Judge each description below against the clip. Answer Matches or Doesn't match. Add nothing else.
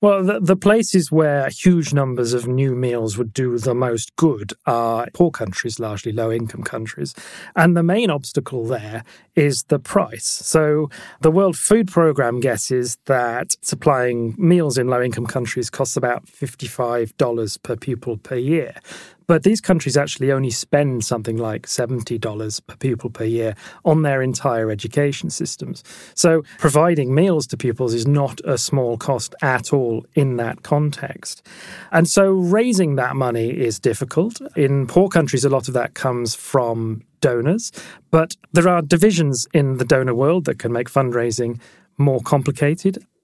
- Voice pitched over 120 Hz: Matches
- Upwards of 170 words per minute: Doesn't match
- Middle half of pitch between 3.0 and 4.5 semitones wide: Doesn't match